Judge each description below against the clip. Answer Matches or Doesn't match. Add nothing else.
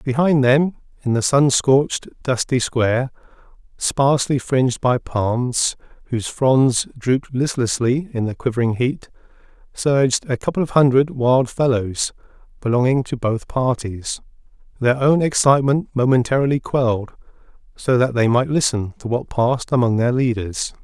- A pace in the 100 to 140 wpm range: Matches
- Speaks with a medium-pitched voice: Doesn't match